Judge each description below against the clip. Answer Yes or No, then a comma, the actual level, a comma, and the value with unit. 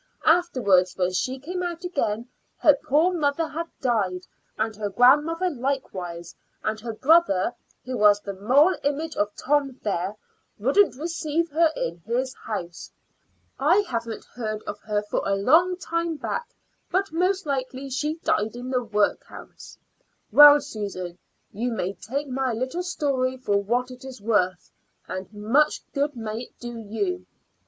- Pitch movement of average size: No, wide, 6.4 semitones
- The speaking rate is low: No, average, 155 wpm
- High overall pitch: Yes, very high, 255 Hz